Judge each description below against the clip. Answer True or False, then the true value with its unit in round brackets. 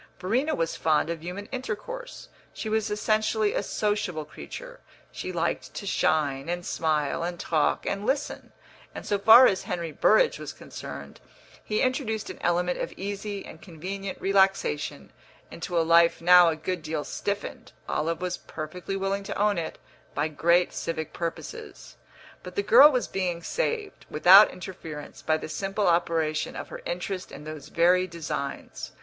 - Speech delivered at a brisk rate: False (160 wpm)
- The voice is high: False (180 Hz)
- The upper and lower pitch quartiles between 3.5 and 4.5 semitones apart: True (4.2 semitones)